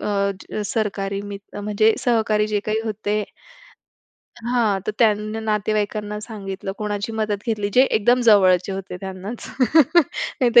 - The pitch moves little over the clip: Yes, narrow, 1.8 semitones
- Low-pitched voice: No, high, 210 Hz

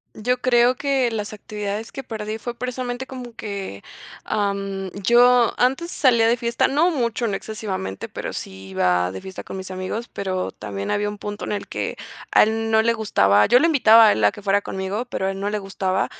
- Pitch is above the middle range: Yes, high, 215 Hz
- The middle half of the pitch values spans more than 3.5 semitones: Yes, average, 3.9 semitones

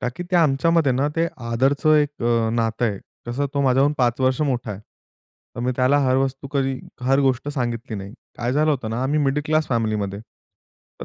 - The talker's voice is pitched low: Yes, low, 130 Hz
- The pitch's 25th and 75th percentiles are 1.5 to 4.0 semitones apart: Yes, average, 3.1 semitones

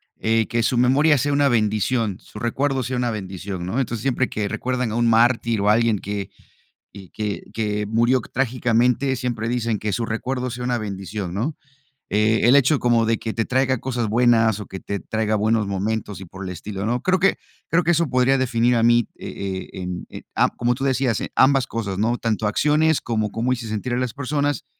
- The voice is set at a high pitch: No, low, 115 Hz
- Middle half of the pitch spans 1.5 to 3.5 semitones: Yes, average, 3.1 semitones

